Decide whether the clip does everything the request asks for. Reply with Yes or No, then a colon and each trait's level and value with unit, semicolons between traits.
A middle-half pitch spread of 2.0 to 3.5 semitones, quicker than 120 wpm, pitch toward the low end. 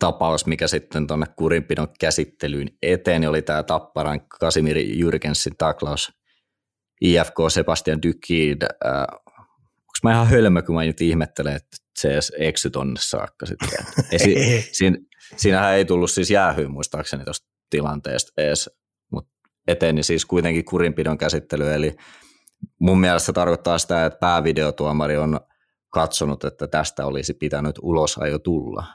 Yes: narrow, 2.5 semitones; average, 145 wpm; very low, 80 Hz